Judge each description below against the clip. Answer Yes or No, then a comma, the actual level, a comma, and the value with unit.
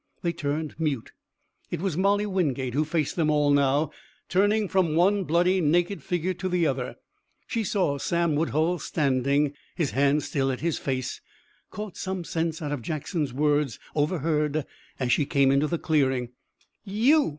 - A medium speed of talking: Yes, average, 160 wpm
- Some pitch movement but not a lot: Yes, average, 4.0 semitones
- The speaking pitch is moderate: Yes, medium, 155 Hz